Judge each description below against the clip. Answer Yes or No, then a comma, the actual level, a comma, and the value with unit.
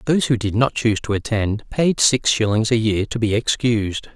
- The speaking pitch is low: Yes, low, 115 Hz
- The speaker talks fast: Yes, fast, 215 wpm